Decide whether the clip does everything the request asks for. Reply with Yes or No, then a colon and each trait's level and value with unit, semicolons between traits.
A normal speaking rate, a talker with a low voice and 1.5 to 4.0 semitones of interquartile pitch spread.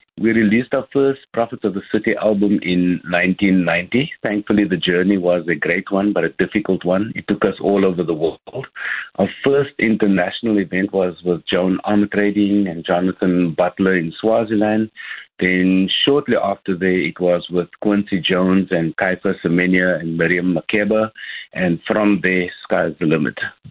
Yes: average, 160 wpm; very low, 95 Hz; average, 2.8 semitones